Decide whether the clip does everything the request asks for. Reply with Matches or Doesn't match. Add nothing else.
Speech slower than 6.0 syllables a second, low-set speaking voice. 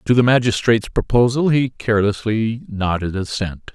Matches